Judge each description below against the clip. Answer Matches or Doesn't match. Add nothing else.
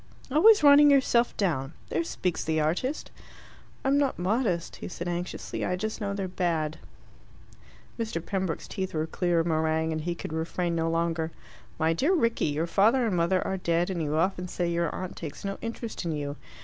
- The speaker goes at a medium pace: Matches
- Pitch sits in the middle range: Matches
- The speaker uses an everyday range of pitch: Matches